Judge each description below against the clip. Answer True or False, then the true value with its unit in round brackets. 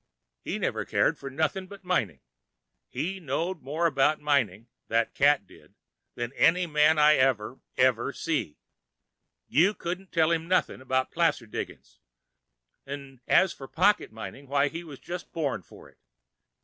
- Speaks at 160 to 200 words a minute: False (150 wpm)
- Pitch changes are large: False (4.5 semitones)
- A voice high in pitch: False (145 Hz)